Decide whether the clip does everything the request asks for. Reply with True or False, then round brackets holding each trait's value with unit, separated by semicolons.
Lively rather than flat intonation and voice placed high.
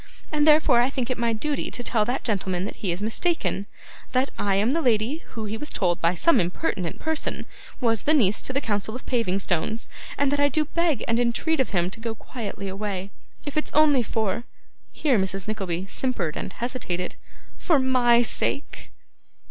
True (5.8 semitones; 230 Hz)